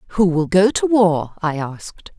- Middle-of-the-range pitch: Yes, medium, 180 Hz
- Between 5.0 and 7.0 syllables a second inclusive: No, 4.5 syllables/s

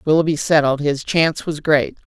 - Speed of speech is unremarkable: Yes, average, 165 wpm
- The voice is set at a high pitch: No, medium, 150 Hz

